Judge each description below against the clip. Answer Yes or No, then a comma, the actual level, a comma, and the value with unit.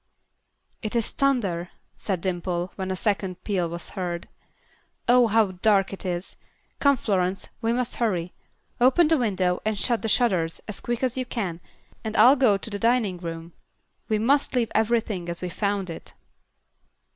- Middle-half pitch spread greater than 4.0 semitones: Yes, average, 4.5 semitones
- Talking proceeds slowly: No, average, 170 wpm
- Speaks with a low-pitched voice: No, high, 205 Hz